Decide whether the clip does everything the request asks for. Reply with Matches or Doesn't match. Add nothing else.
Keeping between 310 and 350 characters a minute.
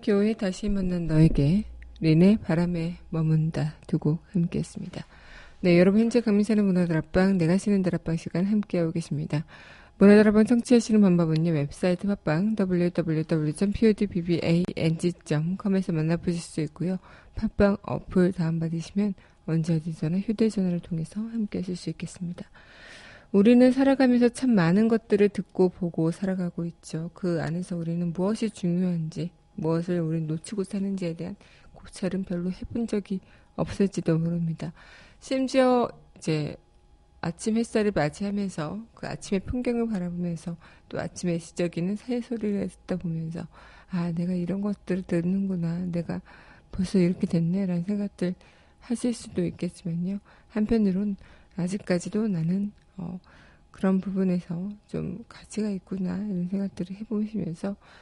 Matches